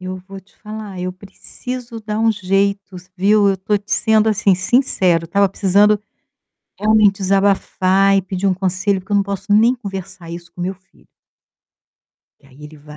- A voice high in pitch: Yes, high, 195 Hz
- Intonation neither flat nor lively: No, narrow, 2.2 semitones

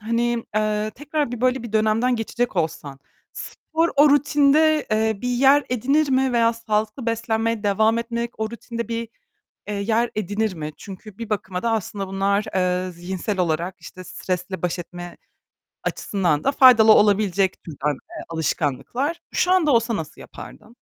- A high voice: Yes, high, 220 Hz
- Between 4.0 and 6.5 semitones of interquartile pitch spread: Yes, average, 4.3 semitones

